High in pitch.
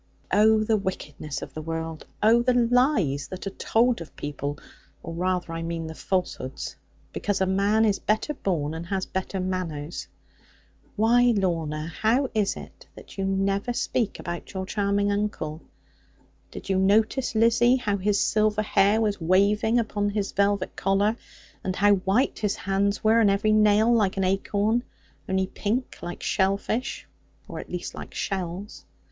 Yes: high, 200 Hz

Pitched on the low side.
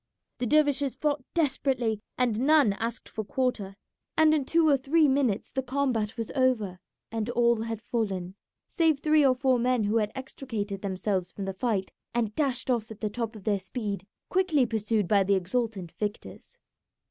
No: high, 235 Hz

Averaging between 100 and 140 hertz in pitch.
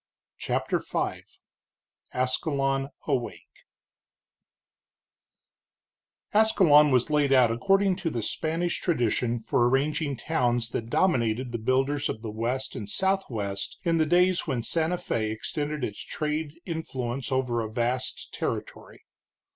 Yes: low, 135 Hz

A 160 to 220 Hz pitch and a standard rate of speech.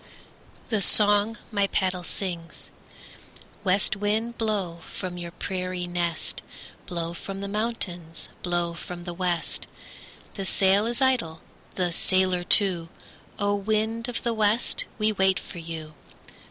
No: high, 190 Hz; slow, 130 wpm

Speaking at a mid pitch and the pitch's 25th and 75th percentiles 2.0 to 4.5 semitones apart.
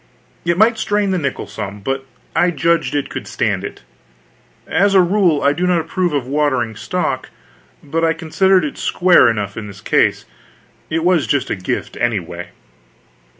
No: medium, 160 Hz; average, 5.2 semitones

